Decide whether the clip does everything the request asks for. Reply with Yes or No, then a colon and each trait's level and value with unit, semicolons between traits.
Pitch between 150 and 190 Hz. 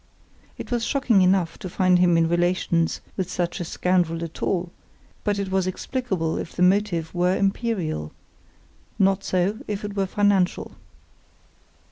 Yes: medium, 185 Hz